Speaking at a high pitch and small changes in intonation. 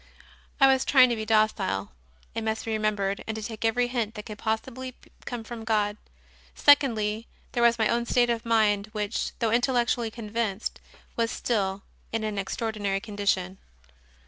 Yes: high, 220 Hz; narrow, 2.1 semitones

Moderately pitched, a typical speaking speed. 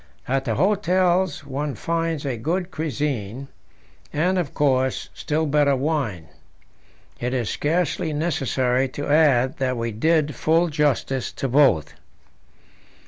No: medium, 145 Hz; slow, 125 wpm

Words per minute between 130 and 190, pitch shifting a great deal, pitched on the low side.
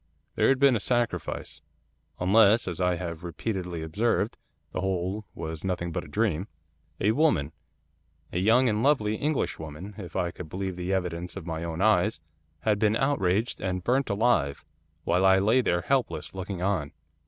No: average, 165 wpm; average, 4.1 semitones; very low, 95 Hz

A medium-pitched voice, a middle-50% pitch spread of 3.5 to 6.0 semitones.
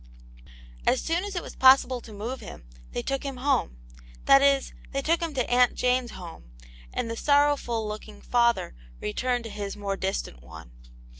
No: high, 245 Hz; average, 4.6 semitones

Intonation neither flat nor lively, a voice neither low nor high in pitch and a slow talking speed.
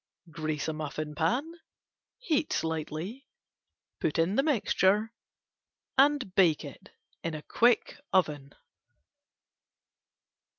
No: wide, 7.7 semitones; medium, 175 Hz; slow, 75 wpm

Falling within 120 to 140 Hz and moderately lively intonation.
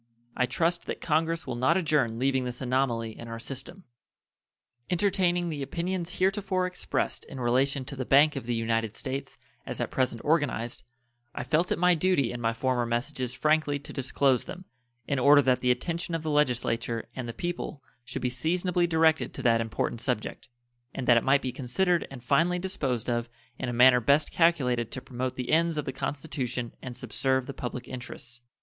Yes: low, 135 Hz; average, 4.7 semitones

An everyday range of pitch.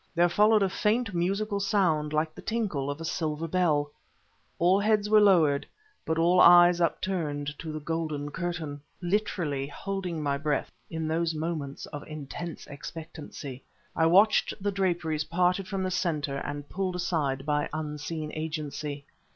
Yes: average, 3.7 semitones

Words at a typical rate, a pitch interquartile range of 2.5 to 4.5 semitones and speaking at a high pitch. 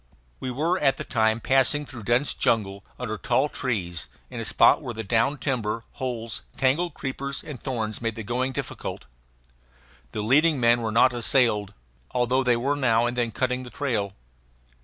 No: average, 175 wpm; average, 2.9 semitones; low, 120 Hz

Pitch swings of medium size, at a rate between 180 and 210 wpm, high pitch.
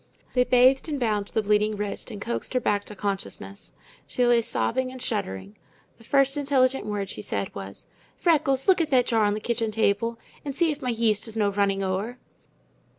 Yes: average, 4.1 semitones; average, 200 wpm; high, 225 Hz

